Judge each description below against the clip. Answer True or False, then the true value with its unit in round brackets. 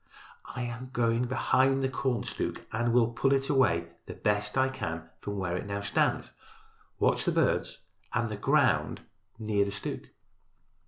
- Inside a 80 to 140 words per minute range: False (165 wpm)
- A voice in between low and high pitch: False (115 Hz)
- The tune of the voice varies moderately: True (4.3 semitones)